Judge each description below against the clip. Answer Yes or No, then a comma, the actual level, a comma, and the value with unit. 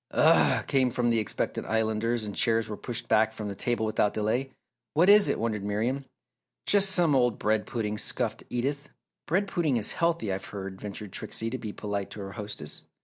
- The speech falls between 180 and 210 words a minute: Yes, average, 190 wpm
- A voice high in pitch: No, low, 110 Hz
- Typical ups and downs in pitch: Yes, average, 4.0 semitones